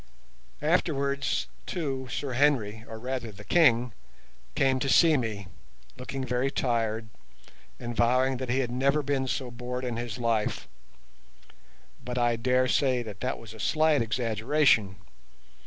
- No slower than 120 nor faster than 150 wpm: Yes, average, 140 wpm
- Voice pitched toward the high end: No, low, 125 Hz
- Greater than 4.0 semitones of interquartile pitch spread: No, average, 2.7 semitones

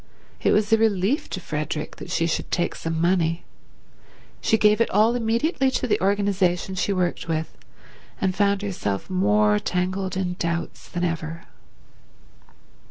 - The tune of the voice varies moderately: Yes, average, 3.8 semitones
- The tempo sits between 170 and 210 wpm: No, average, 150 wpm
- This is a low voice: No, medium, 185 Hz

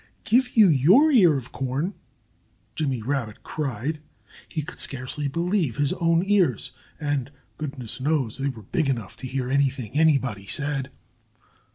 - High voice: No, medium, 140 Hz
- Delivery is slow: No, average, 145 wpm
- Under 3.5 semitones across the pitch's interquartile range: No, average, 3.9 semitones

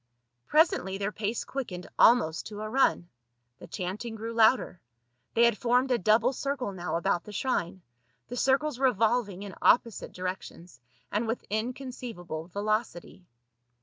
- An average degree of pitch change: Yes, average, 4.7 semitones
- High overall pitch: Yes, high, 215 Hz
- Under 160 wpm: Yes, average, 140 wpm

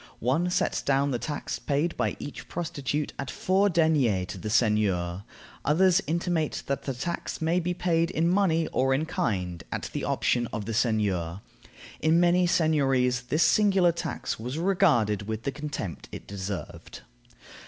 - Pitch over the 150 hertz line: No, medium, 145 Hz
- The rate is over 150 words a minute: Yes, average, 160 wpm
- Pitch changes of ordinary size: No, wide, 7.2 semitones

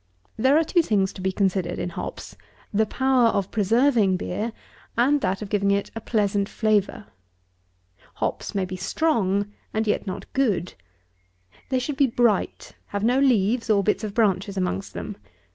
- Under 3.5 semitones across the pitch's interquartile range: No, average, 3.8 semitones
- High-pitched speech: Yes, high, 210 Hz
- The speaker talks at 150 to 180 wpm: Yes, average, 165 wpm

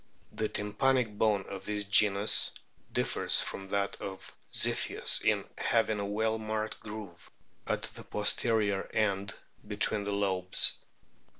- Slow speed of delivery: Yes, slow, 130 wpm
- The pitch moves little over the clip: Yes, narrow, 1.6 semitones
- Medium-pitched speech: No, low, 105 Hz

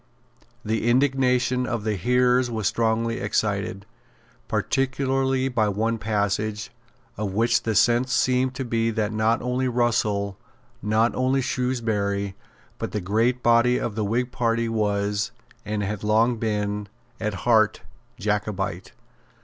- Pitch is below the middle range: Yes, low, 115 Hz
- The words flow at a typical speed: No, slow, 130 wpm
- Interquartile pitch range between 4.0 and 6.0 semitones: No, average, 3.0 semitones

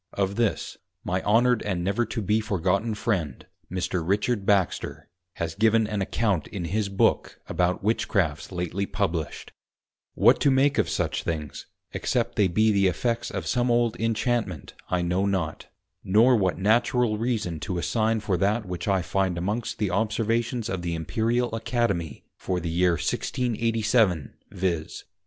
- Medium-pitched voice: No, low, 100 Hz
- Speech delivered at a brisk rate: No, average, 155 wpm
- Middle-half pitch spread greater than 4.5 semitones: No, average, 4.2 semitones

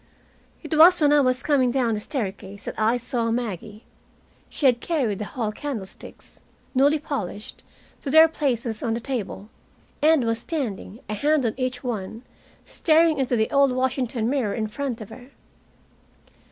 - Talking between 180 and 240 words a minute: No, average, 165 wpm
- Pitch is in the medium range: No, high, 245 Hz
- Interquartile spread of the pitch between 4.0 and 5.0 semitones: Yes, average, 4.4 semitones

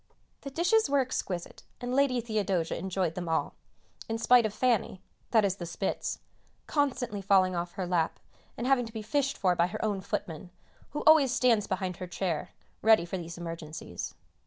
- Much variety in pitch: Yes, wide, 5.8 semitones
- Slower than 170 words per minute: No, average, 180 wpm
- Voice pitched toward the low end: No, high, 200 Hz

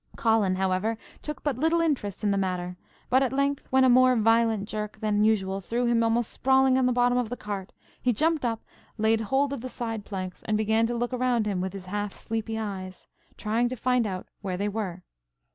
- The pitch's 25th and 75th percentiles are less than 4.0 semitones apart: Yes, average, 3.6 semitones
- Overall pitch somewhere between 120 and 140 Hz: No, high, 225 Hz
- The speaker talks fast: Yes, fast, 215 wpm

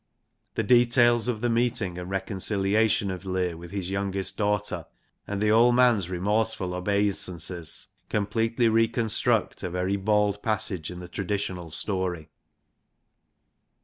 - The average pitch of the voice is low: Yes, low, 100 Hz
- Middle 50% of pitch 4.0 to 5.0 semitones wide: No, average, 3.4 semitones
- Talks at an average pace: No, slow, 125 wpm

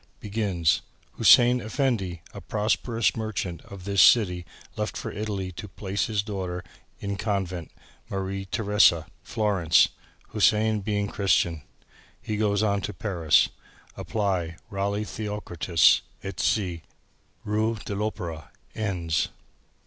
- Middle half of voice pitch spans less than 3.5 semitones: Yes, average, 2.9 semitones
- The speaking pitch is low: Yes, low, 100 Hz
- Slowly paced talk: Yes, slow, 115 wpm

